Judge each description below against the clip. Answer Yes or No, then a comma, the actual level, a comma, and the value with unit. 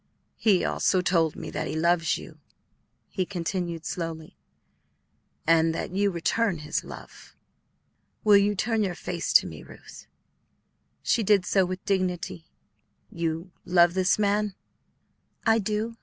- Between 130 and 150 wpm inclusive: Yes, slow, 135 wpm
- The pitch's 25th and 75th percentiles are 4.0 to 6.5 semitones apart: No, average, 3.3 semitones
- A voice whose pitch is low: No, medium, 185 Hz